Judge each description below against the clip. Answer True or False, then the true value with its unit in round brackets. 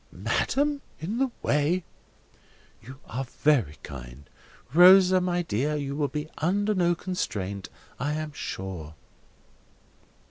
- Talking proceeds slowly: True (110 wpm)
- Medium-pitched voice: True (150 Hz)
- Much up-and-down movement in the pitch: True (8.8 semitones)